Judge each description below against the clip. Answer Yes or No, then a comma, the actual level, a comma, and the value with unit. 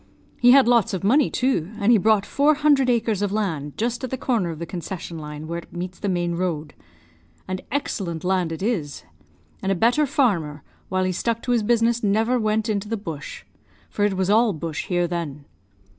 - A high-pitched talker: Yes, high, 200 Hz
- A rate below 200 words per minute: No, fast, 205 wpm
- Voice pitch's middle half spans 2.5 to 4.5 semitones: No, wide, 5.4 semitones